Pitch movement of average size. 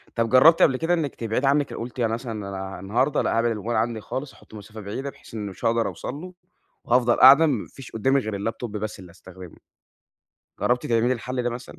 Yes: average, 3.5 semitones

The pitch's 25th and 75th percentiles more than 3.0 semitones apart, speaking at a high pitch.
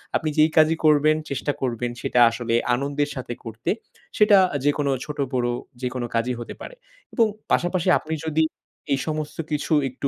No: average, 3.7 semitones; medium, 145 Hz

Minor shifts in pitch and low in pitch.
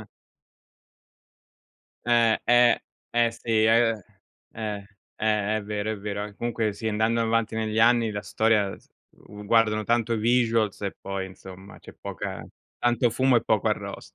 Yes: narrow, 1.9 semitones; low, 110 Hz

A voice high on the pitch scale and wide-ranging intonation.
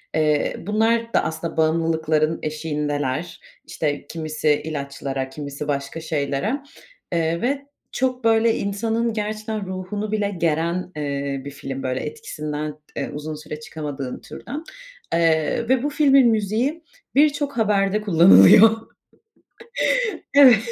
No: medium, 165 Hz; wide, 6.8 semitones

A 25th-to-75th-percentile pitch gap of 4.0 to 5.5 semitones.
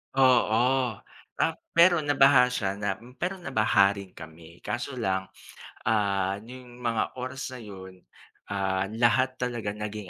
Yes: average, 4.6 semitones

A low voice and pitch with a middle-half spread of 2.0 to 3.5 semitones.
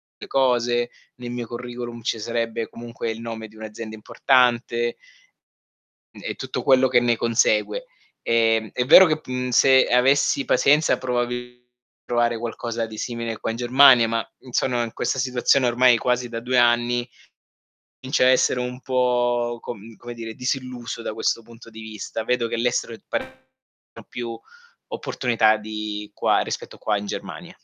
No: low, 120 Hz; narrow, 1.5 semitones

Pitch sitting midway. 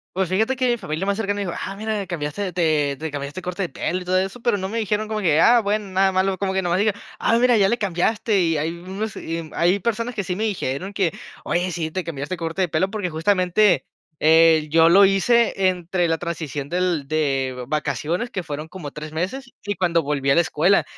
Yes: medium, 180 Hz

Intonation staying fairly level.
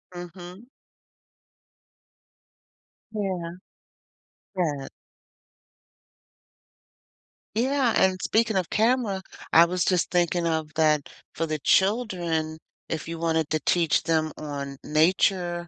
No: average, 3.1 semitones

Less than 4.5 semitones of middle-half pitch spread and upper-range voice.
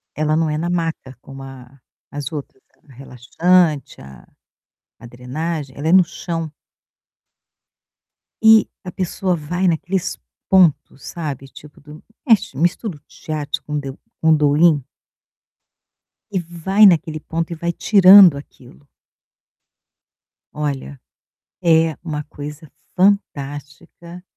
No: average, 3.4 semitones; medium, 155 Hz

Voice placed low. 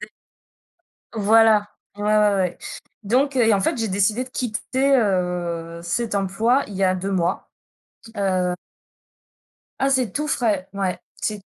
No: high, 205 Hz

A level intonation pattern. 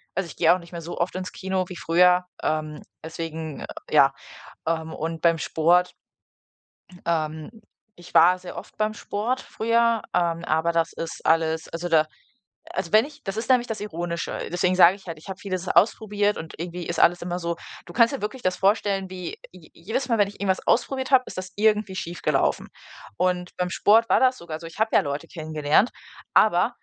No: average, 3.8 semitones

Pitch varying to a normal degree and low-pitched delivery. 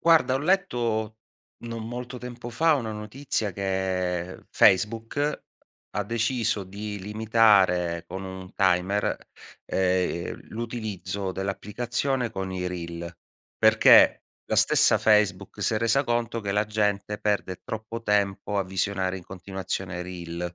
Yes: average, 3.6 semitones; low, 105 Hz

